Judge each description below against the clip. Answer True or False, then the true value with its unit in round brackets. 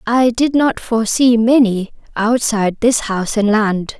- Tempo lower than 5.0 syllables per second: True (4.5 syllables/s)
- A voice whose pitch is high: True (225 Hz)